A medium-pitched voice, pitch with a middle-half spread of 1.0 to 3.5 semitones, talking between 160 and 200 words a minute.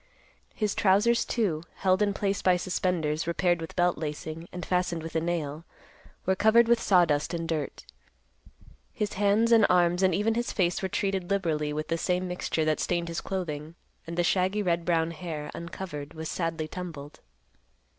Yes: medium, 175 Hz; average, 2.9 semitones; average, 175 wpm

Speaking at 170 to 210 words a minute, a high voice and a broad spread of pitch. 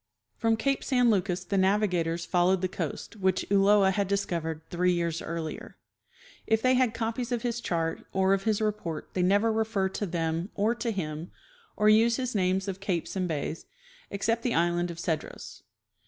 No: average, 180 wpm; high, 195 Hz; average, 4.2 semitones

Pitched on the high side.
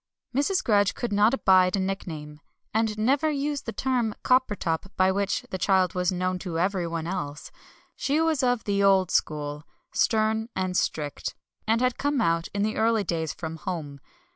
Yes: high, 195 Hz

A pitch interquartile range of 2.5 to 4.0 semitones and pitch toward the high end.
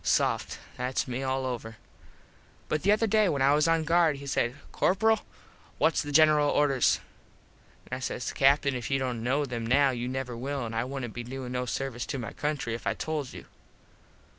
No: average, 3.1 semitones; low, 135 Hz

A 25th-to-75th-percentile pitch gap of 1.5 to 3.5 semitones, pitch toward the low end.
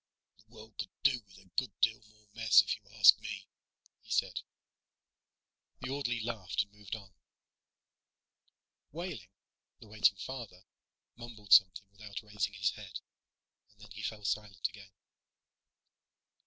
Yes: narrow, 2.6 semitones; low, 105 Hz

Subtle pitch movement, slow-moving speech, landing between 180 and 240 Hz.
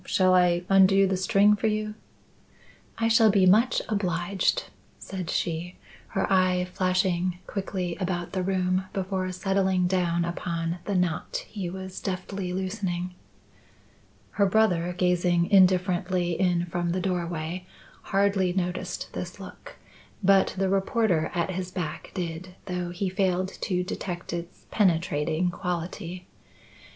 Yes: narrow, 1.6 semitones; slow, 130 wpm; medium, 185 Hz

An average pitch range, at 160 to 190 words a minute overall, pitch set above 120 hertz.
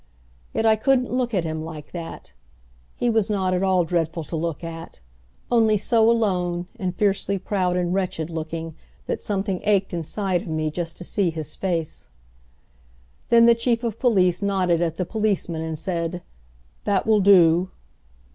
Yes: average, 4.0 semitones; average, 165 wpm; medium, 185 Hz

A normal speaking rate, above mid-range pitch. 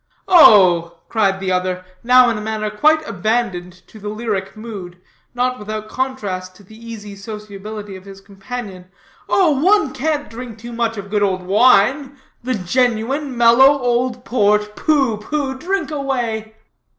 Yes: average, 150 wpm; high, 220 Hz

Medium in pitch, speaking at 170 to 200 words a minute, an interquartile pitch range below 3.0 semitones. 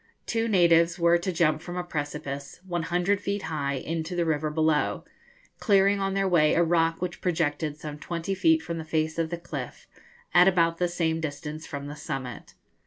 Yes: medium, 165 Hz; average, 185 wpm; narrow, 2.5 semitones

